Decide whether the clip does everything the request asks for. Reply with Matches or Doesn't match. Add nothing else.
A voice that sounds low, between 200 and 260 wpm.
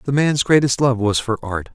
Matches